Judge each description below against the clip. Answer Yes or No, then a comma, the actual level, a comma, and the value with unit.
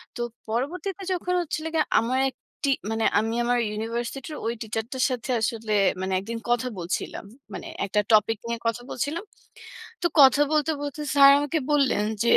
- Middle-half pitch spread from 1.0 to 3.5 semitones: No, average, 4.5 semitones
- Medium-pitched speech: No, high, 245 Hz